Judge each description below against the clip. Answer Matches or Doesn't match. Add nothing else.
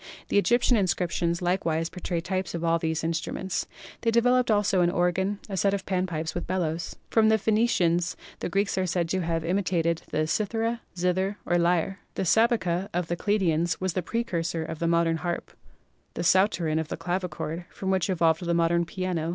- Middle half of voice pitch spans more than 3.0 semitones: Doesn't match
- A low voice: Doesn't match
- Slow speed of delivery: Doesn't match